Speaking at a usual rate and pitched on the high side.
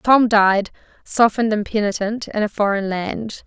Yes: average, 155 wpm; high, 210 Hz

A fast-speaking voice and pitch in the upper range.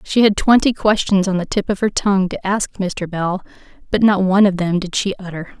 Yes: fast, 235 wpm; high, 195 Hz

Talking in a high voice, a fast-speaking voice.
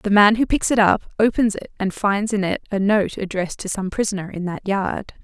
Yes: high, 200 Hz; fast, 240 wpm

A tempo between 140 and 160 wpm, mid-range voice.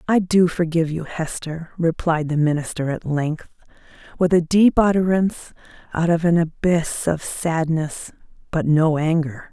Yes: average, 145 wpm; medium, 165 Hz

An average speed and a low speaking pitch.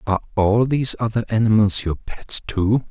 Yes: average, 165 wpm; low, 110 Hz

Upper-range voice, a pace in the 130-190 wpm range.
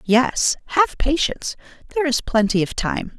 Yes: very high, 270 Hz; average, 150 wpm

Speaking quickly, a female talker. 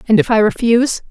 Yes: fast, 220 wpm; female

